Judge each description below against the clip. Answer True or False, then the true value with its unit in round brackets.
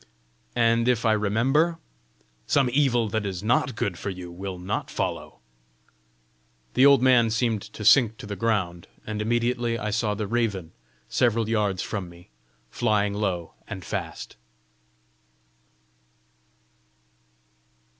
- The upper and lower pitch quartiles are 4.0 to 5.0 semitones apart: False (3.1 semitones)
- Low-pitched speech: True (110 Hz)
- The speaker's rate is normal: False (125 wpm)